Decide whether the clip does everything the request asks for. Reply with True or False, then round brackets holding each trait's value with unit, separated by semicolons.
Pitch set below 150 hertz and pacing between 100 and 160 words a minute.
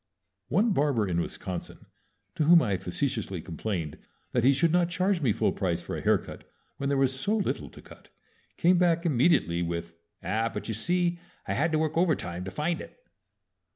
False (140 Hz; 190 wpm)